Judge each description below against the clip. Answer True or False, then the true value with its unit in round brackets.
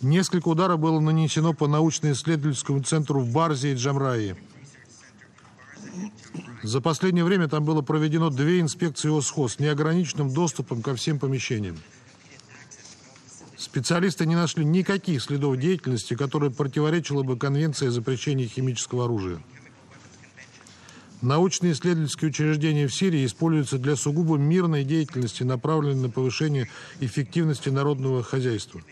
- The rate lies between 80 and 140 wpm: True (115 wpm)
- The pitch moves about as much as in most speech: True (3.7 semitones)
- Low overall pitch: False (145 Hz)